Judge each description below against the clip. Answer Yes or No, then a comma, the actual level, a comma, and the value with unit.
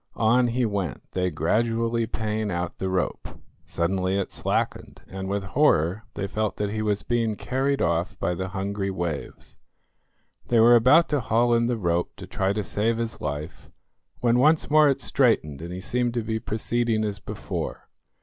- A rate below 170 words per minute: No, average, 180 wpm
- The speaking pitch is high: No, low, 110 Hz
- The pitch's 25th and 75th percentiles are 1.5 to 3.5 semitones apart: No, average, 4.0 semitones